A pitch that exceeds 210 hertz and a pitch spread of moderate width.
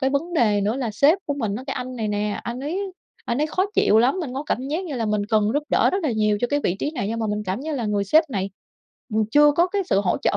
No: very high, 250 Hz; wide, 6.0 semitones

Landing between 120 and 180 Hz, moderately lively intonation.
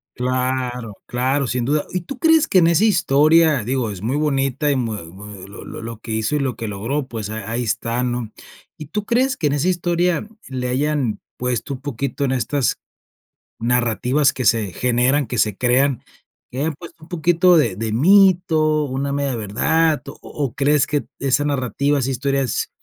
Yes: low, 135 Hz; average, 4.0 semitones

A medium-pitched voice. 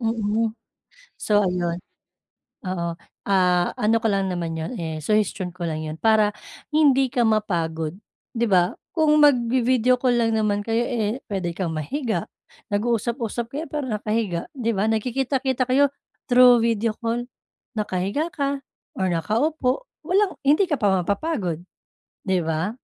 No: high, 220 Hz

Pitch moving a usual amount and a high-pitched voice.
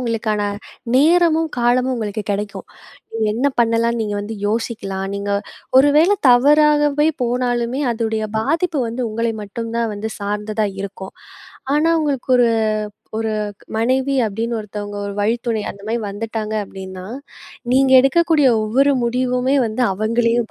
Yes: average, 3.4 semitones; high, 230 Hz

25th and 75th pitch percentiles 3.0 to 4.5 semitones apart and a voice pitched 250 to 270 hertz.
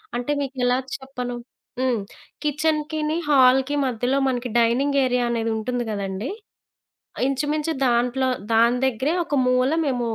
No: narrow, 2.5 semitones; very high, 255 Hz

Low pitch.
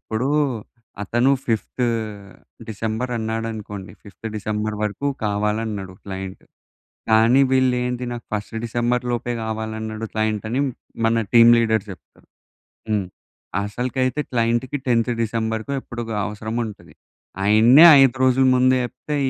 Yes: low, 115 Hz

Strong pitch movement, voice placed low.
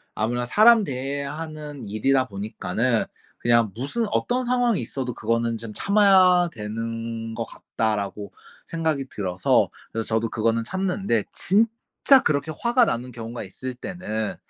Yes: wide, 8.0 semitones; low, 125 Hz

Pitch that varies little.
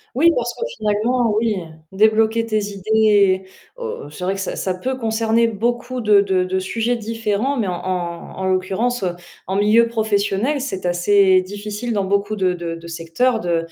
No: average, 3.5 semitones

